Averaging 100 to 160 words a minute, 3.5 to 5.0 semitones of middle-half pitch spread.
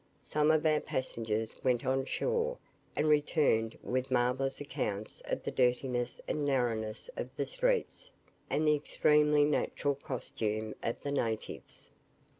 Yes: slow, 135 wpm; average, 4.0 semitones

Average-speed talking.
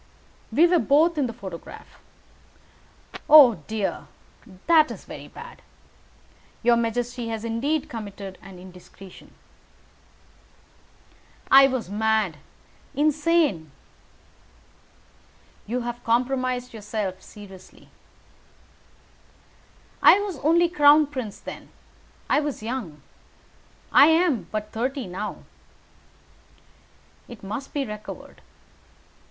No: slow, 95 wpm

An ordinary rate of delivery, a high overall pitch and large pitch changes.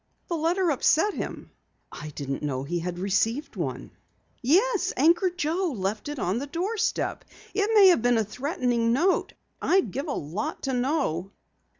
Yes: average, 165 wpm; very high, 275 Hz; wide, 8.9 semitones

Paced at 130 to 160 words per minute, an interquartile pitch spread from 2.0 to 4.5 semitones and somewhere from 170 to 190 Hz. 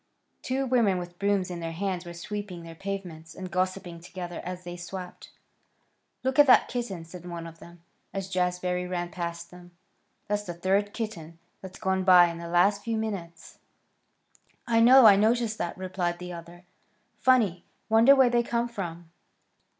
No: average, 170 wpm; average, 3.1 semitones; medium, 185 Hz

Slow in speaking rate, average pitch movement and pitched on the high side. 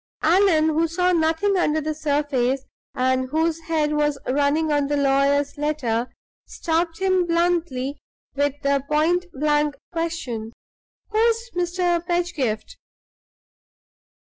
Yes: slow, 115 wpm; average, 3.4 semitones; very high, 310 Hz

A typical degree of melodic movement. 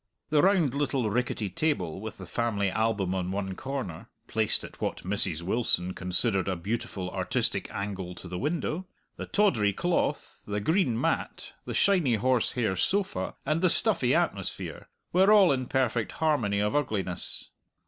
No: wide, 7.4 semitones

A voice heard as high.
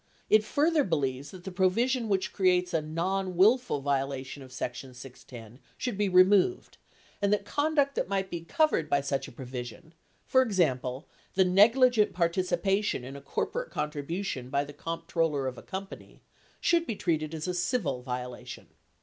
No: medium, 175 Hz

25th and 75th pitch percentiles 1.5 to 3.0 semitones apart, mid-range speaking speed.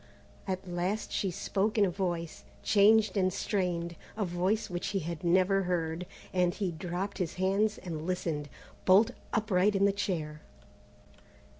Yes: narrow, 2.5 semitones; average, 150 wpm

